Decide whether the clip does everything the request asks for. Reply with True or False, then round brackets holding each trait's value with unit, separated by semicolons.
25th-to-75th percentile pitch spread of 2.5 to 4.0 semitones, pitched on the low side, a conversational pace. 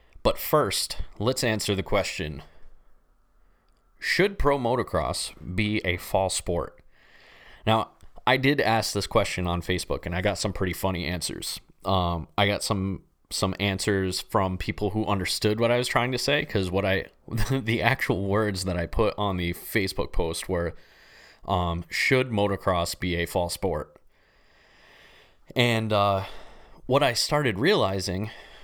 True (3.6 semitones; 95 Hz; 150 wpm)